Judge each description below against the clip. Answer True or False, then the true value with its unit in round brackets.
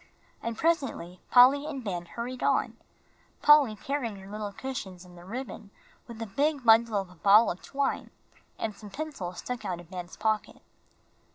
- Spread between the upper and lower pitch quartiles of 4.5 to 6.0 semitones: True (5.6 semitones)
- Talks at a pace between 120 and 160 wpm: False (170 wpm)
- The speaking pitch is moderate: False (225 Hz)